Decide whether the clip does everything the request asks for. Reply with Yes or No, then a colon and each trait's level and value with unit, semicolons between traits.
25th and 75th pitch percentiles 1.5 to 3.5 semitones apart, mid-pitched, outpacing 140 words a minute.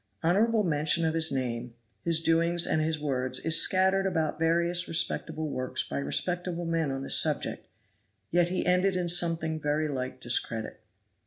Yes: average, 3.1 semitones; medium, 165 Hz; average, 160 wpm